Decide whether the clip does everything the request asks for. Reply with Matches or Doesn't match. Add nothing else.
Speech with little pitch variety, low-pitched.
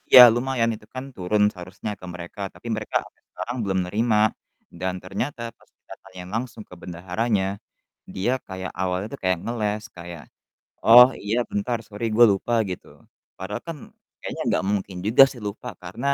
Doesn't match